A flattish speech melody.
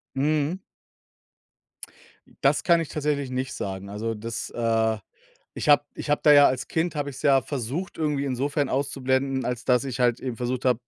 No: average, 3.1 semitones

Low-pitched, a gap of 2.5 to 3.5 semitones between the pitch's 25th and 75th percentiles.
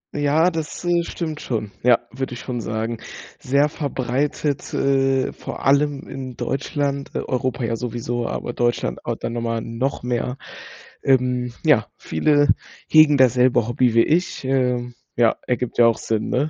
Yes: low, 130 Hz; average, 2.9 semitones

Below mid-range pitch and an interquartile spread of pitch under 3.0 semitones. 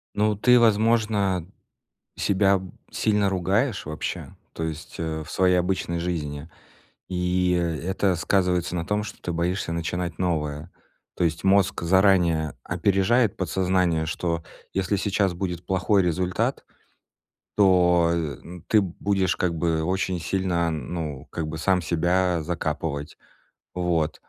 Yes: very low, 90 Hz; narrow, 2.6 semitones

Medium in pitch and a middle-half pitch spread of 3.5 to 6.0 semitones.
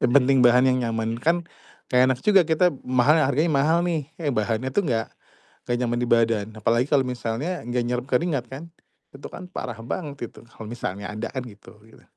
No: low, 125 Hz; average, 4.0 semitones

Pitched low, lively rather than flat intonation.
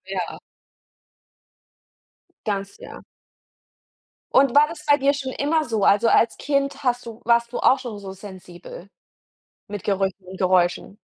No: high, 225 Hz; wide, 6.0 semitones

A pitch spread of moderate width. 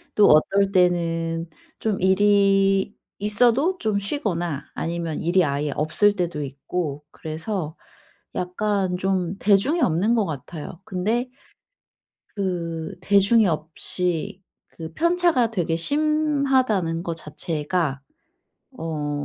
Yes: average, 4.1 semitones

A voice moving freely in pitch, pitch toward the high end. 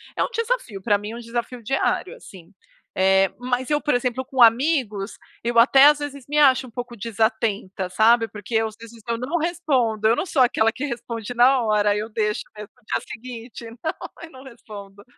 No: average, 3.7 semitones; high, 235 Hz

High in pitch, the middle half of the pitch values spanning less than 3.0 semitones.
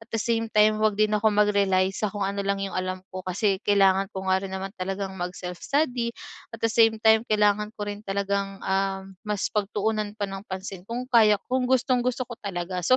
Yes: high, 205 Hz; narrow, 2.4 semitones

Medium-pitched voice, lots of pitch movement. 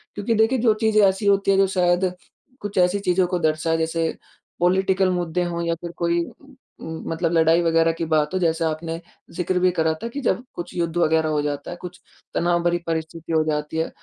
No: medium, 175 Hz; narrow, 2.6 semitones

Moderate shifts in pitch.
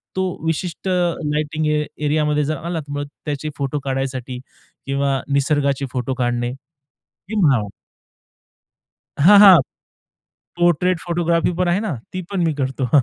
Yes: average, 4.0 semitones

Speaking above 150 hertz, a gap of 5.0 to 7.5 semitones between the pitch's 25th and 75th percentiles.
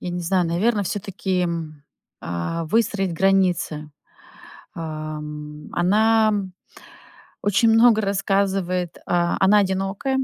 No: high, 190 Hz; average, 3.4 semitones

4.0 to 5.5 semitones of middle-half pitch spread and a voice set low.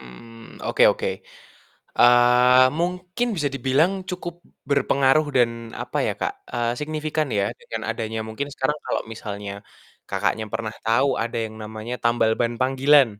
Yes: average, 4.7 semitones; low, 125 Hz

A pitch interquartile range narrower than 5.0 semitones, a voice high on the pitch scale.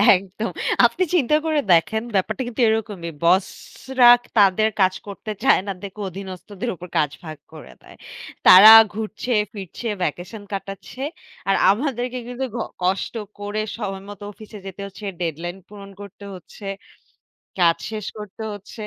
Yes: average, 3.0 semitones; high, 200 Hz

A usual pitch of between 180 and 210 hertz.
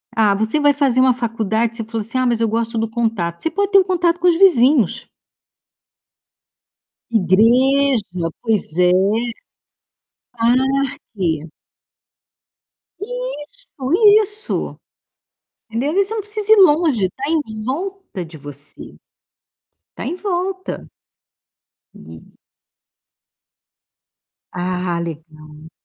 No: high, 235 Hz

